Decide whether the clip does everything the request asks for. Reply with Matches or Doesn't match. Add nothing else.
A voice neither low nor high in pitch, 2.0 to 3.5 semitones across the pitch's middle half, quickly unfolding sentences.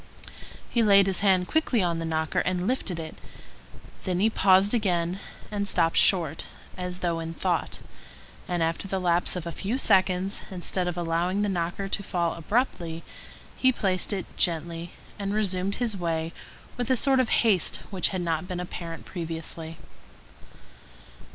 Doesn't match